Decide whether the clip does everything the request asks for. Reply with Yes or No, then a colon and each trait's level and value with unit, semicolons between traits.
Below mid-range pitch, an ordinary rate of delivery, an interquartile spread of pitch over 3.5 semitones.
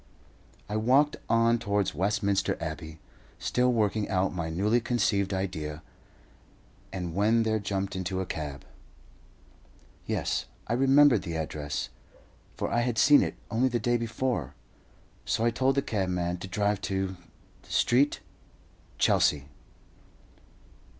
No: low, 100 Hz; slow, 125 wpm; average, 4.5 semitones